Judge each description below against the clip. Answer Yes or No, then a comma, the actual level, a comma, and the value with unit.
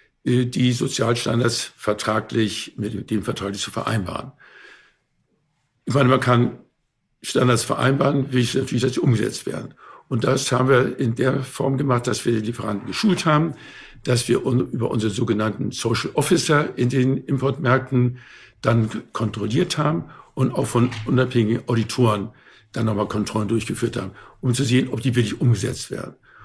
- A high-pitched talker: No, low, 120 Hz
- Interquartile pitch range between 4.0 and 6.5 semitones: No, average, 2.9 semitones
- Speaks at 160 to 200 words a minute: No, average, 145 wpm